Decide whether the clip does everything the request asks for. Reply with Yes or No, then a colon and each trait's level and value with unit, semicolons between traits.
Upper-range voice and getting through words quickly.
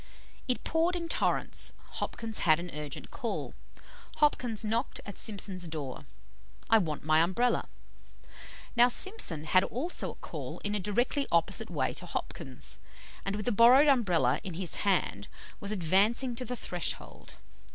No: high, 205 Hz; average, 150 wpm